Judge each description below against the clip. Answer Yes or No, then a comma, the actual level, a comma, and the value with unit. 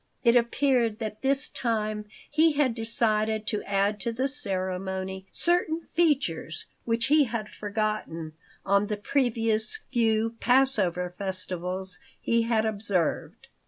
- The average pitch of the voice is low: No, high, 220 Hz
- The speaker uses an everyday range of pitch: Yes, average, 3.8 semitones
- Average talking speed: No, slow, 125 wpm